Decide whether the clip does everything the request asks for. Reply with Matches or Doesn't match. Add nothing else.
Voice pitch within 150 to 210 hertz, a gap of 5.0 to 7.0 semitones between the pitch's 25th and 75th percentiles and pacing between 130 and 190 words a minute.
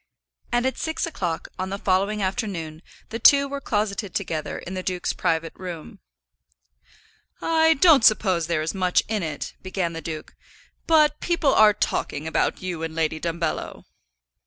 Matches